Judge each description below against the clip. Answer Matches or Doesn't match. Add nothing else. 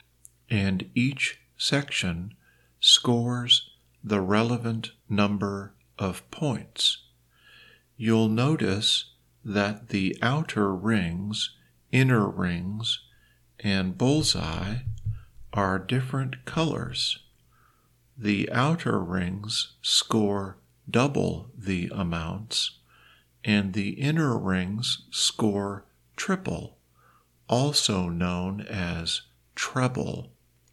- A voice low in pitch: Matches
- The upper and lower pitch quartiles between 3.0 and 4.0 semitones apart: Doesn't match